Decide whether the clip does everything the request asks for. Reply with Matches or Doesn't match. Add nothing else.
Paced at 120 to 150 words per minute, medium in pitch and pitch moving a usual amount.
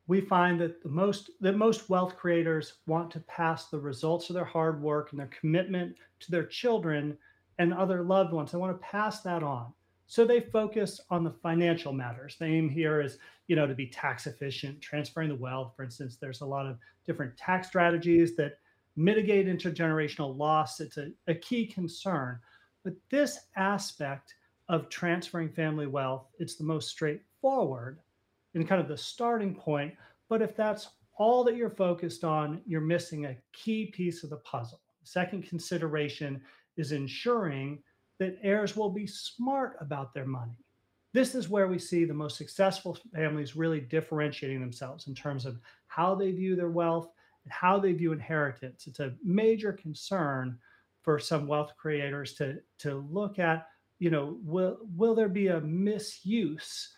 Doesn't match